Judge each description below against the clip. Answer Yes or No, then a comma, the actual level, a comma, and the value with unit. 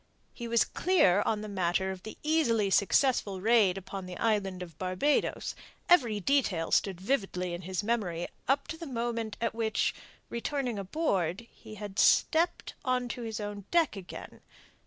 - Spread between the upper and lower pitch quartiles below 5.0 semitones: Yes, average, 4.4 semitones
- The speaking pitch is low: No, high, 215 Hz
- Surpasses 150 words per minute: Yes, average, 160 wpm